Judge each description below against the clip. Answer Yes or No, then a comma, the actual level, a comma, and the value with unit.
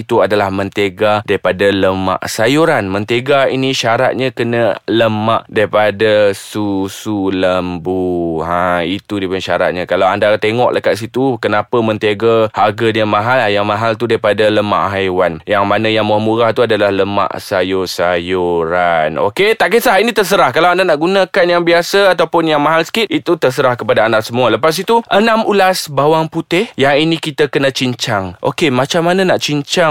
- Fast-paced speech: Yes, fast, 160 wpm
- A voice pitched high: No, low, 110 Hz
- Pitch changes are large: Yes, wide, 7.3 semitones